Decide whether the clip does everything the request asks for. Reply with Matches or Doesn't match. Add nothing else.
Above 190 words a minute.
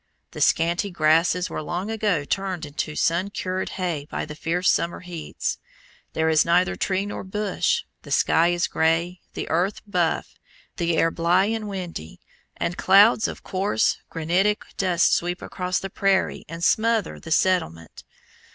Doesn't match